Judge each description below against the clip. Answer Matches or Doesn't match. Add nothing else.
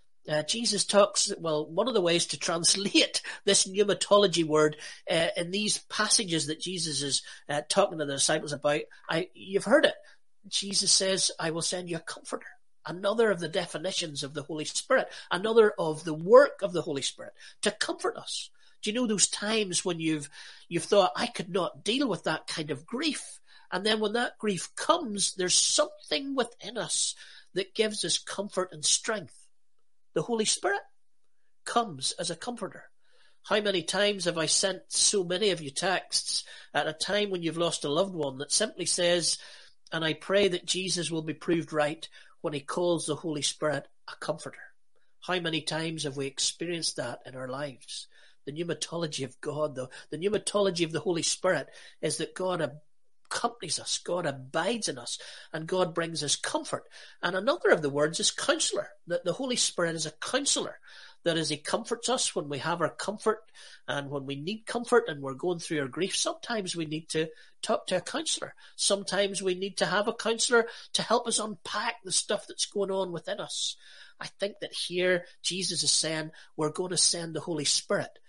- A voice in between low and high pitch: Matches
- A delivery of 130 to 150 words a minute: Doesn't match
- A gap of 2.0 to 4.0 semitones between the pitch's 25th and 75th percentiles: Doesn't match